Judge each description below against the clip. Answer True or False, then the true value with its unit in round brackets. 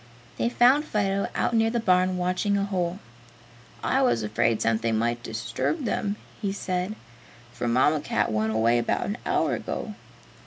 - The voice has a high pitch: False (180 Hz)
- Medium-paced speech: True (160 wpm)